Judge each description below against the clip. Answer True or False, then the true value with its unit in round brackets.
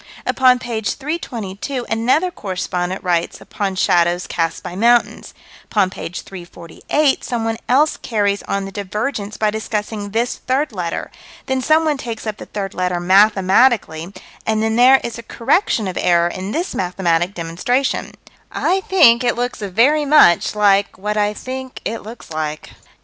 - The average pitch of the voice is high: True (215 Hz)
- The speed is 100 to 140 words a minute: False (150 wpm)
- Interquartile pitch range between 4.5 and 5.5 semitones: True (5.0 semitones)